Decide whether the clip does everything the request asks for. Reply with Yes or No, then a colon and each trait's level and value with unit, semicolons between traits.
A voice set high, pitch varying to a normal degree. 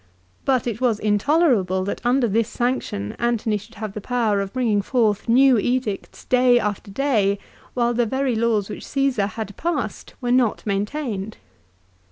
Yes: high, 230 Hz; average, 3.5 semitones